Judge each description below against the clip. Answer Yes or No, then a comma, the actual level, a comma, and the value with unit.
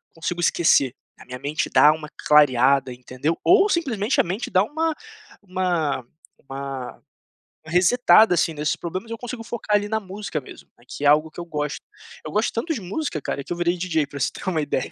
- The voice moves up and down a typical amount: No, wide, 6.4 semitones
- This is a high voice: No, medium, 170 Hz